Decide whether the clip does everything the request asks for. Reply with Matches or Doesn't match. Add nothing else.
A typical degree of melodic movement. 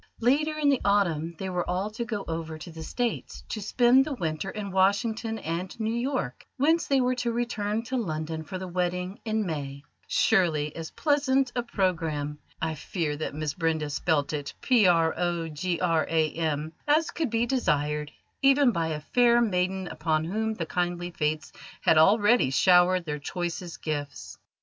Doesn't match